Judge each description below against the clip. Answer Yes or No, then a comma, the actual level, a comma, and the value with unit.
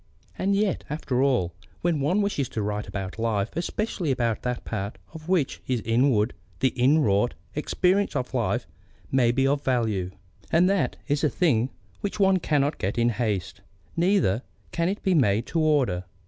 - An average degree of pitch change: No, wide, 6.8 semitones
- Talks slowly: No, average, 175 wpm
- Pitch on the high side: No, low, 135 Hz